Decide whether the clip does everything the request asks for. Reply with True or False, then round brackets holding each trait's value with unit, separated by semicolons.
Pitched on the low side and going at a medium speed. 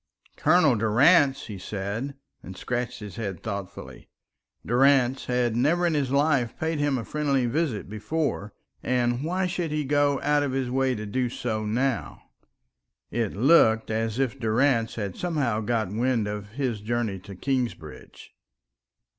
True (125 Hz; 150 wpm)